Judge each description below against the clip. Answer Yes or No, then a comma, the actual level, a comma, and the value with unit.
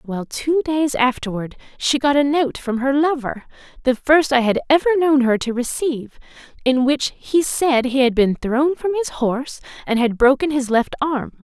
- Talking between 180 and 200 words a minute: Yes, average, 185 wpm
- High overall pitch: Yes, very high, 270 Hz